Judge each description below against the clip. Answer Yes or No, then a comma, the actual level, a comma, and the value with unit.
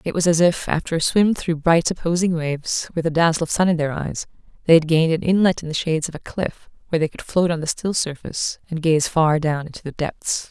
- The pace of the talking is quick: Yes, fast, 255 wpm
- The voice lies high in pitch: No, medium, 165 Hz